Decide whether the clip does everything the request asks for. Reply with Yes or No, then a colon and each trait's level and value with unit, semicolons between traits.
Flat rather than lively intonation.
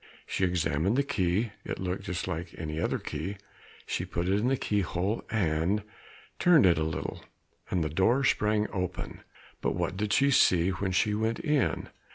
No: average, 3.8 semitones